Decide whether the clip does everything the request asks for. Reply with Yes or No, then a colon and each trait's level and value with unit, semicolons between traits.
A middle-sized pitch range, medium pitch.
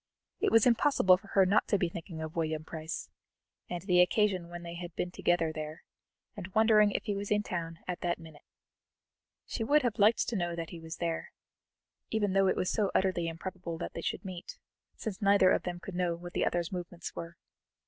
Yes: average, 3.0 semitones; medium, 180 Hz